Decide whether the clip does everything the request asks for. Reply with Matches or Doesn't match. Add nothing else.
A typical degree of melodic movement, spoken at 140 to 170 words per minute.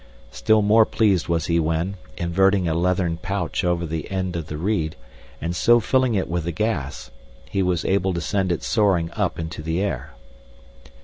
Doesn't match